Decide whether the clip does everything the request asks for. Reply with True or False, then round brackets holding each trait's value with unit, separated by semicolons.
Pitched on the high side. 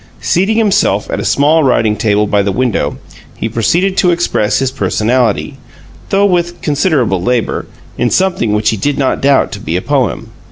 False (130 Hz)